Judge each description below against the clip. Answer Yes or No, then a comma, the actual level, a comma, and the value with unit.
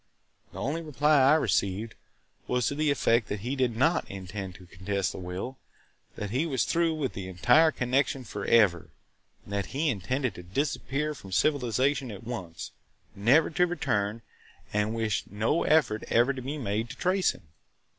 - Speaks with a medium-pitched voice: No, low, 120 Hz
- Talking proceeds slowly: No, average, 165 wpm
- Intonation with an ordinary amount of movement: No, wide, 6.0 semitones